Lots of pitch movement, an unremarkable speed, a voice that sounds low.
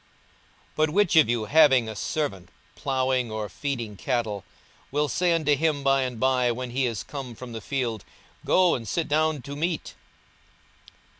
No: average, 4.3 semitones; average, 170 wpm; low, 130 Hz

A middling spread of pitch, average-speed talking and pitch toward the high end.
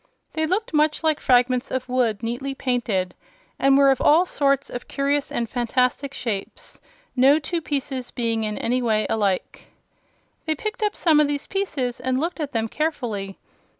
Yes: average, 4.0 semitones; average, 170 wpm; very high, 265 Hz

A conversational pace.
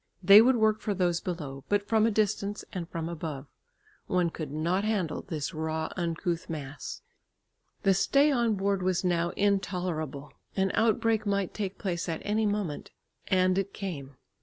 Yes: average, 160 wpm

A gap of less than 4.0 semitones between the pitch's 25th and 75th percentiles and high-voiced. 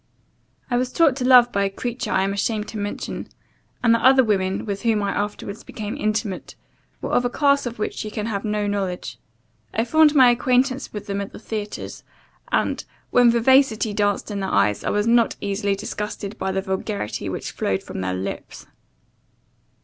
Yes: average, 3.3 semitones; high, 210 Hz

